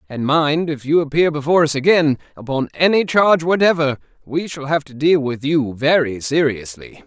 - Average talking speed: Yes, average, 180 wpm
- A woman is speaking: No, male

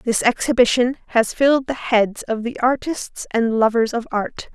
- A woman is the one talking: Yes, female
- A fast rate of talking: No, average, 170 wpm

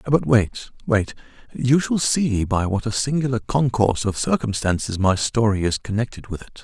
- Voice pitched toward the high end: No, low, 115 Hz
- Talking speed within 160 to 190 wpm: Yes, average, 165 wpm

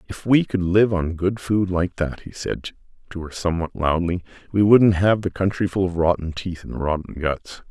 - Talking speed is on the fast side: Yes, fast, 210 wpm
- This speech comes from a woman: No, male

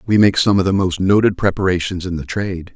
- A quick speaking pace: Yes, fast, 240 wpm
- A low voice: Yes, very low, 95 Hz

